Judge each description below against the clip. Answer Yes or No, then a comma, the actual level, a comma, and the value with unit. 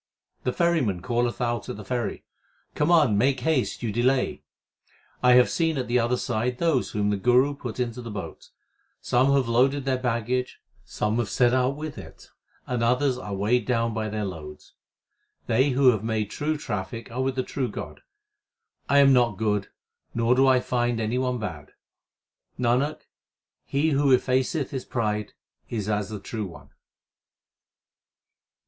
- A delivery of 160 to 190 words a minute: Yes, average, 165 wpm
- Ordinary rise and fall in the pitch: Yes, average, 3.3 semitones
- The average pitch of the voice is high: No, low, 125 Hz